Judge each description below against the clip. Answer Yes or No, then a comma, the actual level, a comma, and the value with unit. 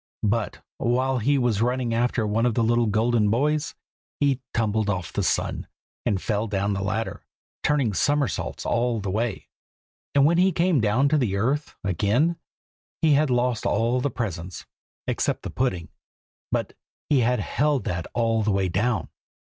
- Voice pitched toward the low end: Yes, low, 115 Hz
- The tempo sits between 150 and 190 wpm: Yes, average, 165 wpm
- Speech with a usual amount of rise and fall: Yes, average, 4.1 semitones